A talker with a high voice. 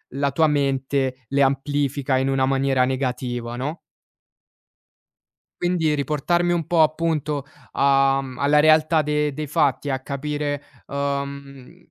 No: medium, 140 Hz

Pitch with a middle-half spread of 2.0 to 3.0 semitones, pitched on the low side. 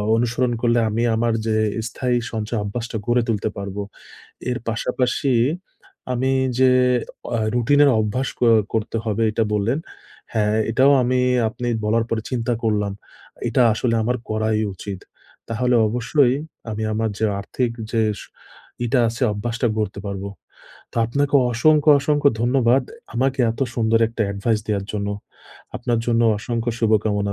Yes: narrow, 2.4 semitones; low, 115 Hz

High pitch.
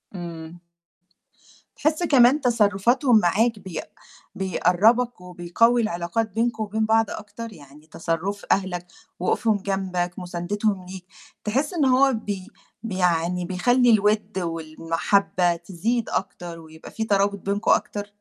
Yes: high, 200 Hz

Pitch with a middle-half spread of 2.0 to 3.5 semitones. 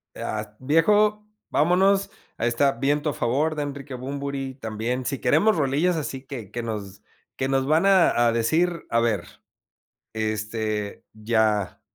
No: wide, 5.5 semitones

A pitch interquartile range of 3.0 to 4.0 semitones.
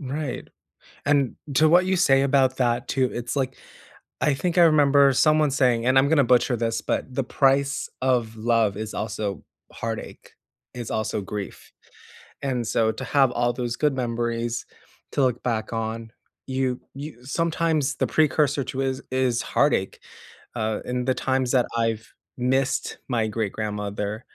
Yes: average, 3.3 semitones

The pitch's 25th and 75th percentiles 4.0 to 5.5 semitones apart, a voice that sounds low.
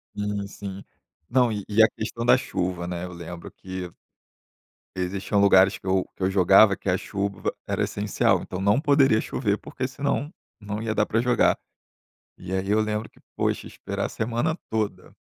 No: average, 2.9 semitones; low, 100 Hz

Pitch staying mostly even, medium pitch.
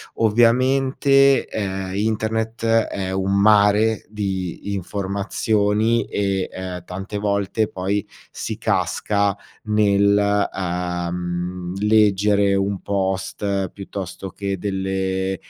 No: narrow, 1.9 semitones; low, 100 Hz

